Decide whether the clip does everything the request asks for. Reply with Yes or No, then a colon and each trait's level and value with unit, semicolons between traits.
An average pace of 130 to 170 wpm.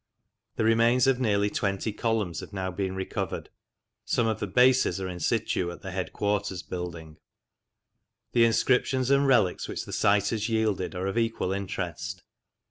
Yes: average, 160 wpm